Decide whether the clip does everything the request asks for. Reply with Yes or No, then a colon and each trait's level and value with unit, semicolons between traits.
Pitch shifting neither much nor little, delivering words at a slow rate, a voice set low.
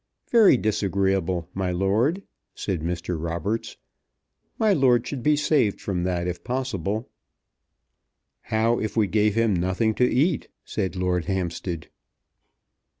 Yes: average, 5.0 semitones; slow, 125 wpm; low, 100 Hz